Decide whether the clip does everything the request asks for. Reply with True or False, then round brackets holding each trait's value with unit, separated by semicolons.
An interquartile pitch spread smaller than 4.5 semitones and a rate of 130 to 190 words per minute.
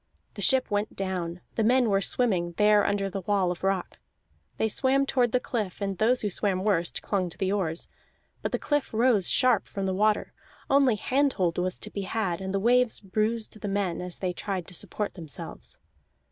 False (3.4 semitones; 200 wpm)